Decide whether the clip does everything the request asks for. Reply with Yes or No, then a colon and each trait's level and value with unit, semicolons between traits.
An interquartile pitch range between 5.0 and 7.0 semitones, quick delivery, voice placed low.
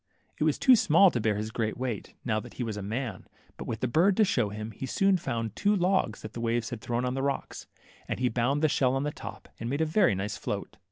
Yes: average, 5.3 semitones; fast, 270 wpm; low, 125 Hz